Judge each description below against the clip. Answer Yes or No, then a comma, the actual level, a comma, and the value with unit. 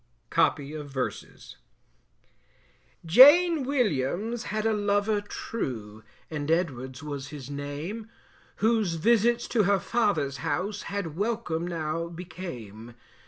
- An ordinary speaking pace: No, slow, 110 wpm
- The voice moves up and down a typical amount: No, wide, 7.1 semitones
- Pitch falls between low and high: Yes, medium, 175 Hz